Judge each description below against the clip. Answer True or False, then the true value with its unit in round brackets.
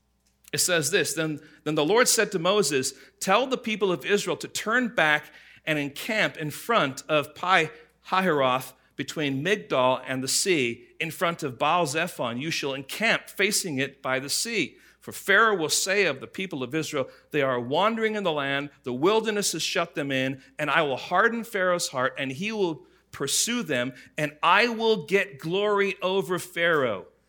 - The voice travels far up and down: True (6.0 semitones)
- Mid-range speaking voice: True (155 Hz)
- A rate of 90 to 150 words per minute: False (180 wpm)